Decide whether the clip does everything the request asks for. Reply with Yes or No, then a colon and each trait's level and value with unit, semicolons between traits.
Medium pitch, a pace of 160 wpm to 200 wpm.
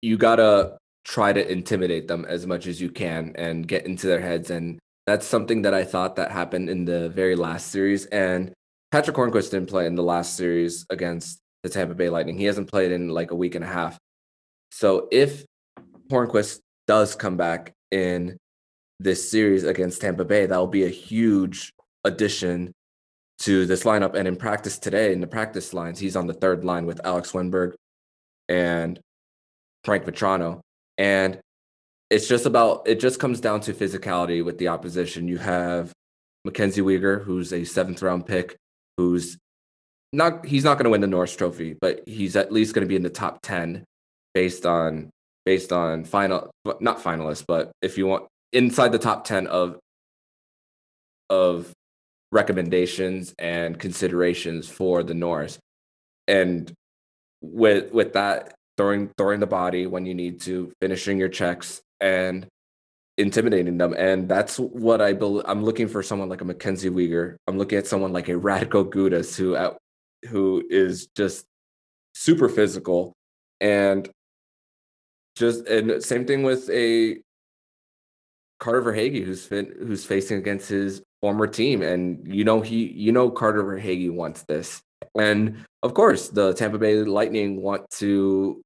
No: very low, 90 Hz; average, 165 wpm